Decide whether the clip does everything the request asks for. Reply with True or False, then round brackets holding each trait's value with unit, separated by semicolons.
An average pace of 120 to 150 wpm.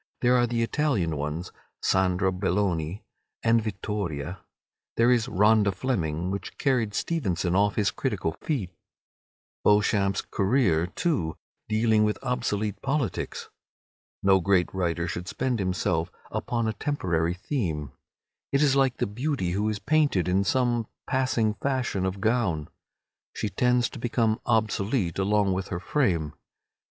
True (135 wpm)